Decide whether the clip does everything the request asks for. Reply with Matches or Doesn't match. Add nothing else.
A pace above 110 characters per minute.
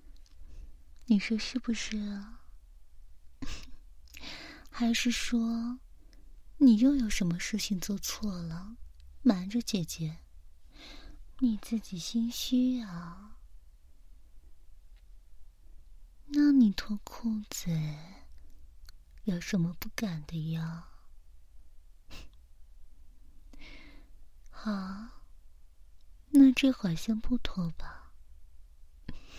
Doesn't match